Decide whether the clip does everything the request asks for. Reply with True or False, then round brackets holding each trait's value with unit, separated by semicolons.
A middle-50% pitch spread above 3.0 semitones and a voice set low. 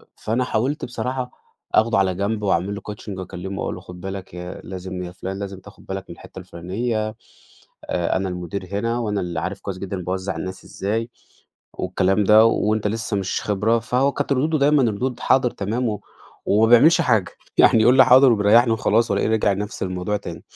True (3.5 semitones; 105 Hz)